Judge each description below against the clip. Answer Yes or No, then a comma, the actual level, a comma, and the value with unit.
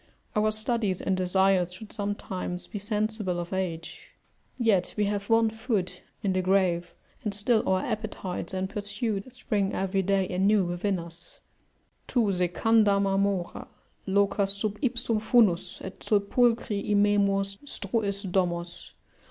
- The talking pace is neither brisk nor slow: No, slow, 130 wpm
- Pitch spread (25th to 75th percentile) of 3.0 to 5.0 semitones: No, narrow, 2.4 semitones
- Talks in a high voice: Yes, high, 200 Hz